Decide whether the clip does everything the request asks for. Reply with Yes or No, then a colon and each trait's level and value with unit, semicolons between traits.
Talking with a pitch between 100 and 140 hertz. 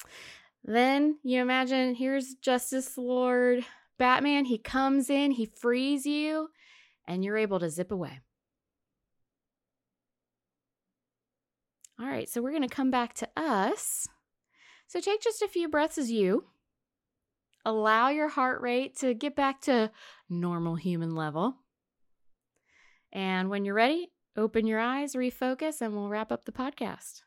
No: very high, 255 Hz